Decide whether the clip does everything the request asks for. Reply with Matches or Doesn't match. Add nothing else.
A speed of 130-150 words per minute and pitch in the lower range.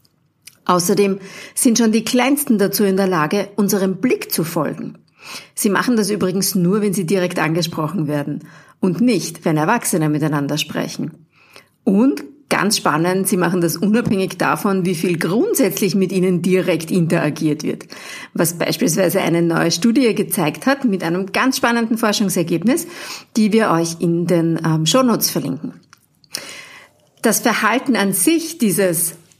Doesn't match